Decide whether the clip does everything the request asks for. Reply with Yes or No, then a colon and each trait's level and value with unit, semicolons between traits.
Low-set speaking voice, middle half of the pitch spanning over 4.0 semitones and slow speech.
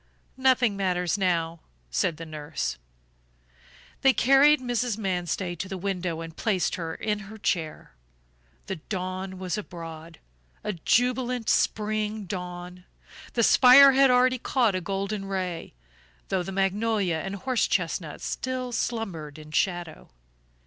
No: high, 195 Hz; average, 4.6 semitones; slow, 130 wpm